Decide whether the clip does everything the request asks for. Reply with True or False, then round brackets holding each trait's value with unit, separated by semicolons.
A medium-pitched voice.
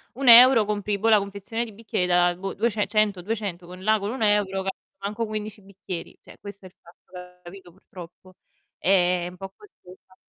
False (195 Hz)